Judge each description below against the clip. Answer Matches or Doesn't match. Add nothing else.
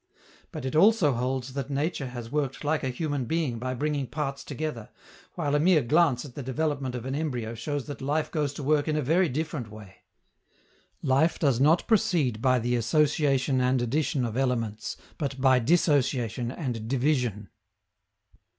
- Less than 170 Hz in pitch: Matches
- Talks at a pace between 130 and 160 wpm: Doesn't match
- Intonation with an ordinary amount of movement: Matches